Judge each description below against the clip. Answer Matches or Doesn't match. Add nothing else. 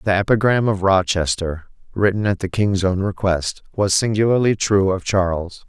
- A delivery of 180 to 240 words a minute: Doesn't match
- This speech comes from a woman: Doesn't match